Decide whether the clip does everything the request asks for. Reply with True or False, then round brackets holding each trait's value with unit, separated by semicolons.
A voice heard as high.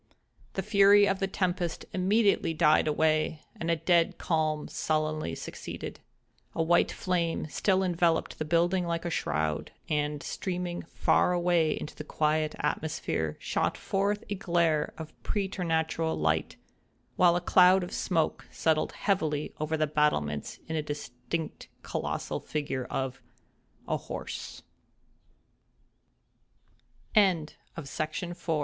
False (165 Hz)